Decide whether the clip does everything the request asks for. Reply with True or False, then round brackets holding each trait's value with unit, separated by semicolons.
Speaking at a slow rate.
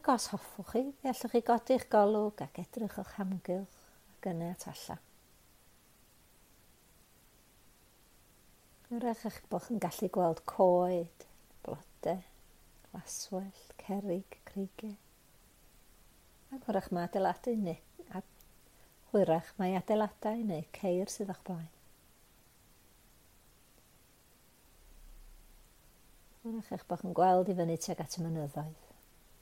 True (105 wpm)